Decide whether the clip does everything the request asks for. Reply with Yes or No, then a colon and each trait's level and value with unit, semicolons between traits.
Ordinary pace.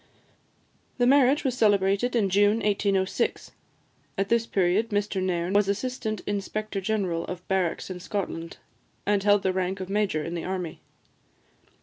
Yes: average, 145 wpm